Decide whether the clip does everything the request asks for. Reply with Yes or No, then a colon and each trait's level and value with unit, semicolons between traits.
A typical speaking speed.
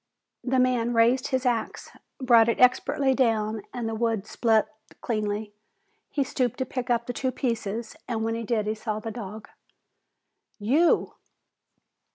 Yes: average, 155 wpm